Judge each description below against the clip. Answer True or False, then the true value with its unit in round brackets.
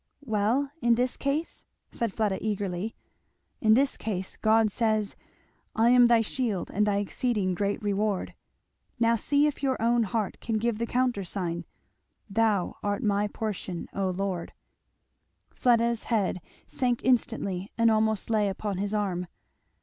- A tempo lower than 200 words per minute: True (140 wpm)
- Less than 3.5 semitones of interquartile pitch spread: True (2.8 semitones)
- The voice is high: True (215 Hz)